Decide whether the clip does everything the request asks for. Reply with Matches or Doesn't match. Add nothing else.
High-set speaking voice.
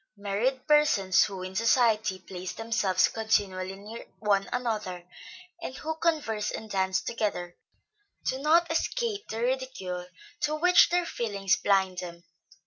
Matches